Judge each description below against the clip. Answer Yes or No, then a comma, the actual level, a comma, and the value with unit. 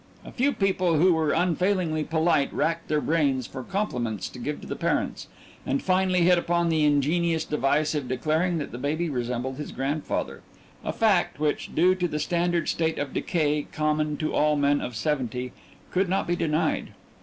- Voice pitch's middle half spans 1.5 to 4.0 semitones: Yes, average, 3.3 semitones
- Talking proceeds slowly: No, average, 180 wpm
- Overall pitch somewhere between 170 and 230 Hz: No, medium, 155 Hz